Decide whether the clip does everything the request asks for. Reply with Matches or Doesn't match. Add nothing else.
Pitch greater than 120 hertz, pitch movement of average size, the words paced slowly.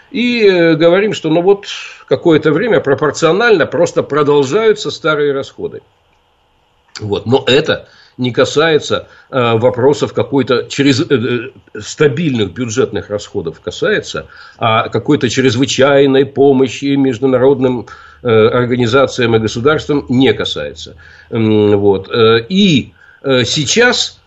Doesn't match